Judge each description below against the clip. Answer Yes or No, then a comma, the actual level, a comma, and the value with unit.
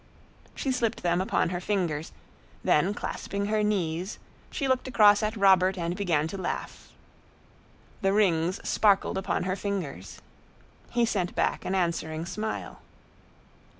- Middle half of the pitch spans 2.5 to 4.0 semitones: Yes, average, 3.3 semitones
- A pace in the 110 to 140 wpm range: Yes, slow, 135 wpm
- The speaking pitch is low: No, high, 190 Hz